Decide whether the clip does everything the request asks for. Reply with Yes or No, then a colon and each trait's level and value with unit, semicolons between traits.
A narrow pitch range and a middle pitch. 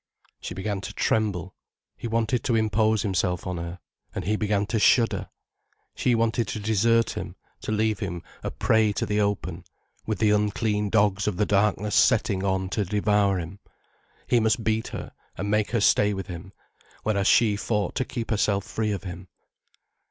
No: narrow, 2.1 semitones; low, 105 Hz